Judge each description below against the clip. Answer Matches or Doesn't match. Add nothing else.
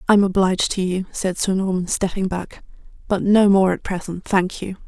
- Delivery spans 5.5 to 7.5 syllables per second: Doesn't match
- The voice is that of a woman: Matches